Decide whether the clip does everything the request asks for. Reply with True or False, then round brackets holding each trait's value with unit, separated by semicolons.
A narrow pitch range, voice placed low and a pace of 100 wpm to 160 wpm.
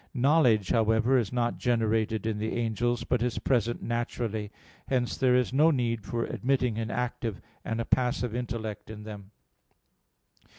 True (2.0 semitones; 115 Hz; 155 wpm)